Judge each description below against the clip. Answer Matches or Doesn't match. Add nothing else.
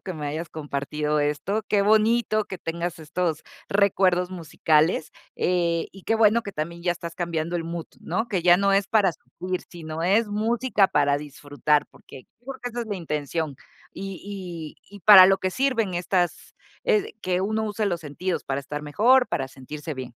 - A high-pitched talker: Doesn't match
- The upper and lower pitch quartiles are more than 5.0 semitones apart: Doesn't match